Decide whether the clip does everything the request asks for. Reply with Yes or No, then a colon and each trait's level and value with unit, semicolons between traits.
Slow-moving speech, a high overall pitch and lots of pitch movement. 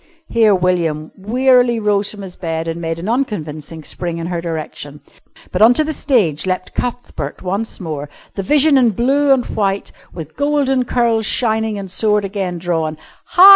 No: average, 175 wpm; high, 200 Hz; wide, 6.3 semitones